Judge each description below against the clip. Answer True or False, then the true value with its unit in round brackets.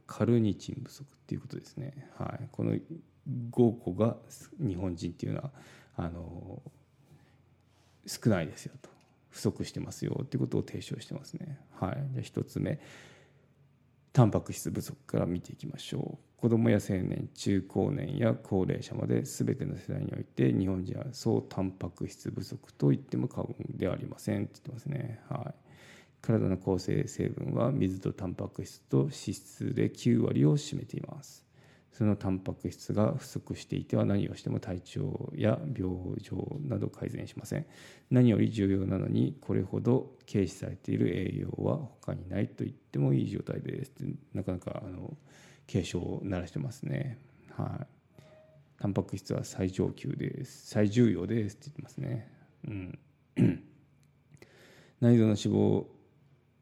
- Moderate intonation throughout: False (6.1 semitones)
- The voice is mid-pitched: False (120 Hz)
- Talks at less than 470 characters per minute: True (305 characters per minute)